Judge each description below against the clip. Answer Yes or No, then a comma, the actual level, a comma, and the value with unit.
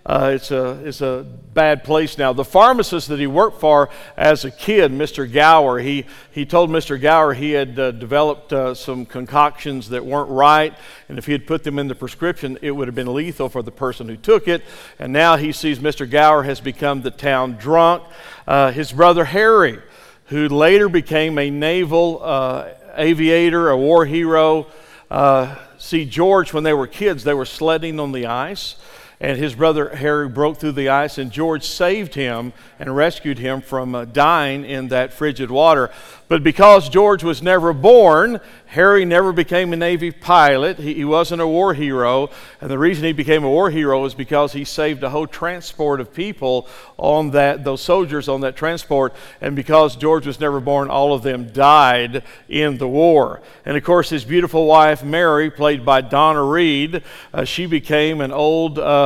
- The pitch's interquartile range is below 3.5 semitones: Yes, average, 2.9 semitones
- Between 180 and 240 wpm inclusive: Yes, average, 190 wpm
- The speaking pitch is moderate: Yes, medium, 150 Hz